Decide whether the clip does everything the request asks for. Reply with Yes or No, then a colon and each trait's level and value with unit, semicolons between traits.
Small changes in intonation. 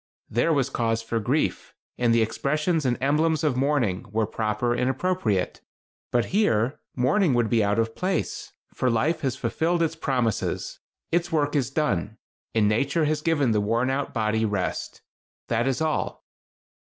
No: average, 5.3 semitones